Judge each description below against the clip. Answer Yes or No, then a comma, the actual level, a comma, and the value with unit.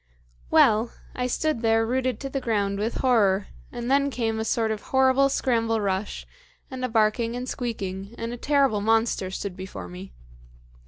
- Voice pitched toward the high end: Yes, high, 225 Hz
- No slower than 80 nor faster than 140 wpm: No, average, 170 wpm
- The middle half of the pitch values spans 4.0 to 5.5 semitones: No, average, 3.6 semitones